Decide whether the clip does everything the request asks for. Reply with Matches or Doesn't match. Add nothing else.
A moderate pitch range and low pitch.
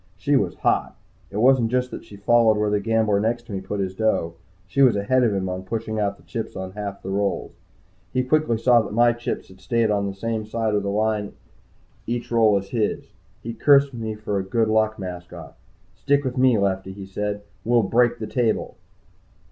Matches